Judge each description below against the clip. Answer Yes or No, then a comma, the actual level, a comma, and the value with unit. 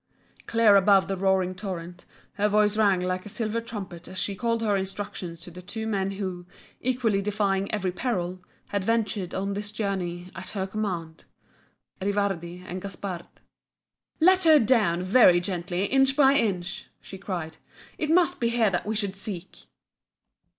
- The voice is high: Yes, high, 195 Hz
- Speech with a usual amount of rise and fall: Yes, average, 3.0 semitones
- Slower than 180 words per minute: Yes, average, 160 wpm